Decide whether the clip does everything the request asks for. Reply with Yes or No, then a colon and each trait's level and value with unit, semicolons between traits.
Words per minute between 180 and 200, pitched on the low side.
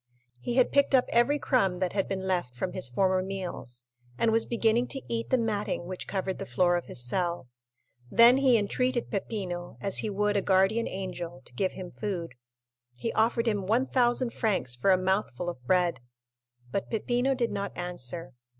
No: average, 185 wpm; high, 195 Hz